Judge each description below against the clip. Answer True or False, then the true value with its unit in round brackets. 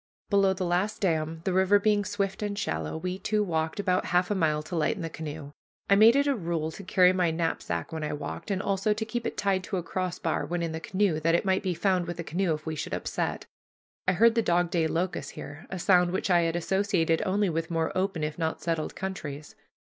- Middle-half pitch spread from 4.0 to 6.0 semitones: False (3.3 semitones)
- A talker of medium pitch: True (180 Hz)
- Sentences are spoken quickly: True (240 wpm)